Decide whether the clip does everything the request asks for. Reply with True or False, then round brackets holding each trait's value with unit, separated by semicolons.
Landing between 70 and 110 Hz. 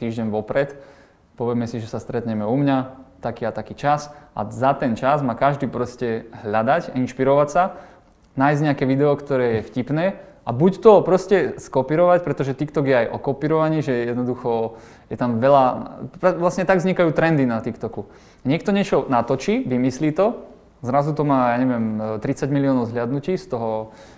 False (135 Hz)